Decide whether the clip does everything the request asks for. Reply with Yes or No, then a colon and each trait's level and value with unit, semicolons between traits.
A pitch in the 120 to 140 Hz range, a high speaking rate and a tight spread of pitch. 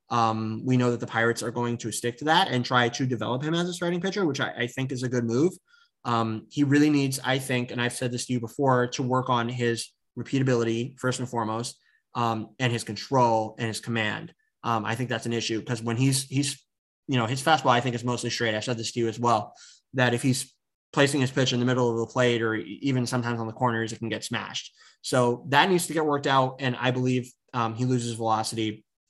Yes: low, 125 Hz; fast, 245 wpm; narrow, 2.2 semitones